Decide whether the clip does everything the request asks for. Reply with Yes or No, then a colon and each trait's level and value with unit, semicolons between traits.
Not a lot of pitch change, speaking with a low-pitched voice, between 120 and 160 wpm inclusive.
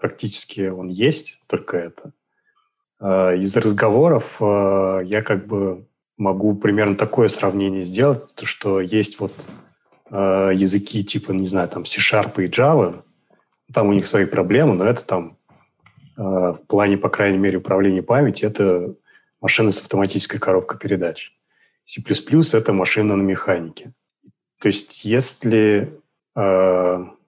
Yes: narrow, 2.0 semitones; low, 100 Hz; average, 125 wpm